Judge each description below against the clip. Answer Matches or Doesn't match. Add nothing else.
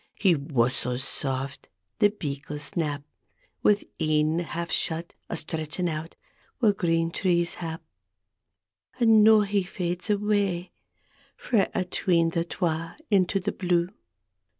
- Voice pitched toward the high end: Doesn't match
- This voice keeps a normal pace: Doesn't match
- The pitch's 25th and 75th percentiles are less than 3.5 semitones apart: Doesn't match